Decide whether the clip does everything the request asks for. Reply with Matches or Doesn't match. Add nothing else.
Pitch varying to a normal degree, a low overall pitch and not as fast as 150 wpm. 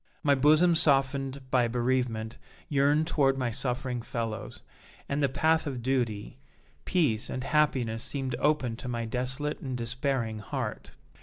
Matches